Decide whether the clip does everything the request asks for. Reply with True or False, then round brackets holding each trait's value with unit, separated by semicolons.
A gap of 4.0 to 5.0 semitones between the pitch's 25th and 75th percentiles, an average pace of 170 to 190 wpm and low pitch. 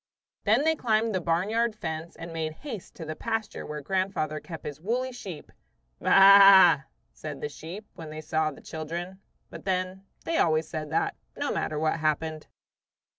False (4.3 semitones; 175 wpm; 170 Hz)